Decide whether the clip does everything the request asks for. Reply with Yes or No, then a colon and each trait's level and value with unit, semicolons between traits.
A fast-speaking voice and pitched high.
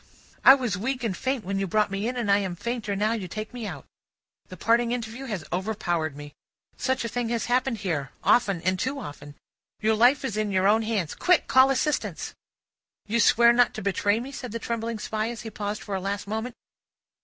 Yes: fast, 215 wpm; high, 220 Hz